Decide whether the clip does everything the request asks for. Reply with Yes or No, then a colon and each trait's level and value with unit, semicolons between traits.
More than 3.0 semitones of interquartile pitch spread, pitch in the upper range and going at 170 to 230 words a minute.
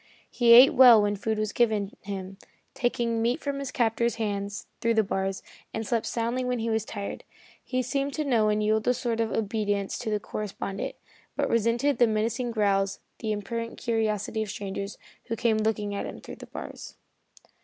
No: narrow, 2.4 semitones; high, 220 Hz; average, 190 wpm